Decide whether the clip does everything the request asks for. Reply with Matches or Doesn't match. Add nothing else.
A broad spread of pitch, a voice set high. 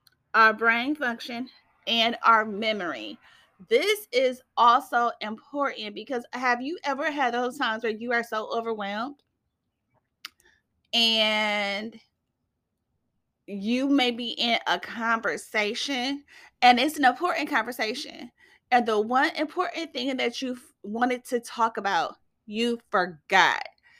Doesn't match